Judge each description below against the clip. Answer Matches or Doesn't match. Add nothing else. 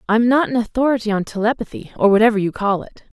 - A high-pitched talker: Matches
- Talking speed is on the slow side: Doesn't match